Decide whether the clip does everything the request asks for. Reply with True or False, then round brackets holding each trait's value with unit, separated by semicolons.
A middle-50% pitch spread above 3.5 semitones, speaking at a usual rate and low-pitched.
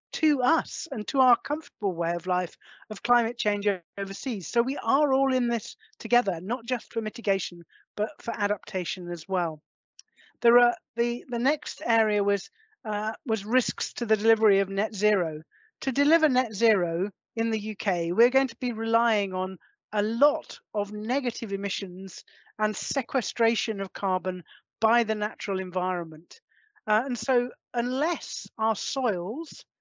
False (4.0 semitones; 155 wpm; 220 Hz)